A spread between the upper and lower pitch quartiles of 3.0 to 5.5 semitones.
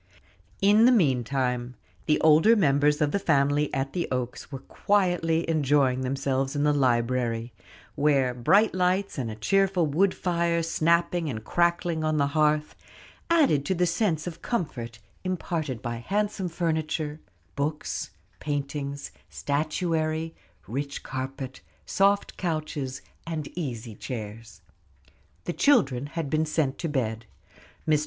Yes: average, 4.3 semitones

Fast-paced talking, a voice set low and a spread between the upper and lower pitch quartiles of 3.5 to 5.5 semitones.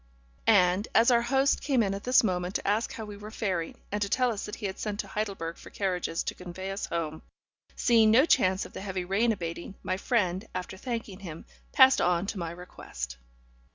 No: fast, 215 wpm; high, 200 Hz; average, 3.8 semitones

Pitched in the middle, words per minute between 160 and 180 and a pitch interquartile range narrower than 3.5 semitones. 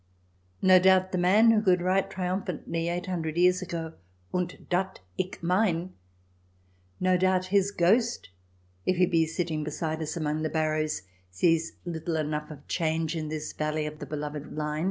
Yes: medium, 165 Hz; average, 175 wpm; average, 3.1 semitones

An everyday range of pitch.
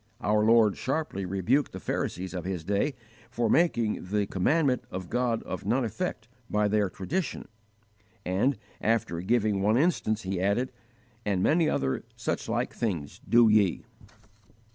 Yes: average, 4.2 semitones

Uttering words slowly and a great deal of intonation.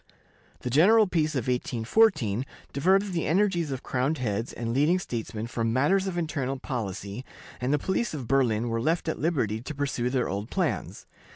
No: average, 175 wpm; wide, 6.2 semitones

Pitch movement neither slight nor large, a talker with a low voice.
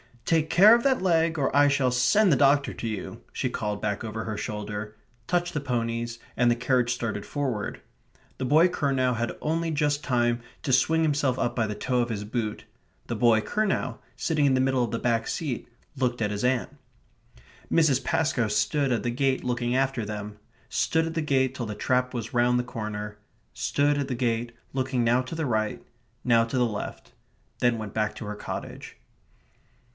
Yes: average, 3.8 semitones; low, 125 Hz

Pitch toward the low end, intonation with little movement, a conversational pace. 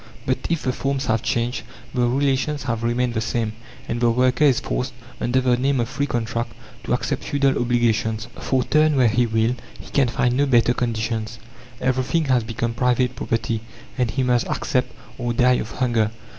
Yes: low, 125 Hz; narrow, 1.9 semitones; average, 185 wpm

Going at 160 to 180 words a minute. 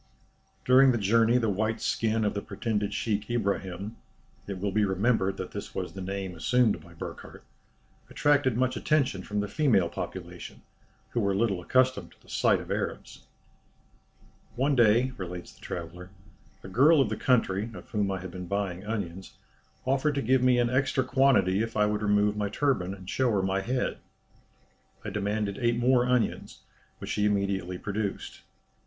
Yes: average, 175 wpm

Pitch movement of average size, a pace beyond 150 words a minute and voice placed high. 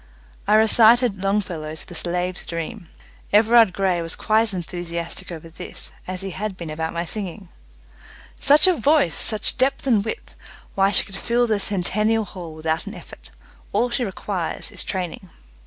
Yes: average, 4.1 semitones; average, 165 wpm; high, 195 Hz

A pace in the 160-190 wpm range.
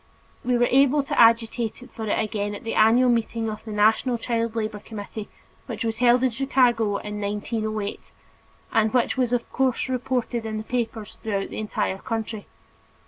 Yes: average, 170 wpm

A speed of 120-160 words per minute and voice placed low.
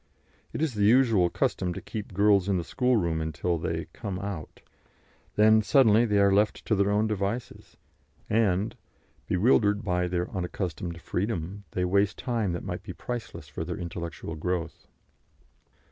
Yes: average, 155 wpm; low, 100 Hz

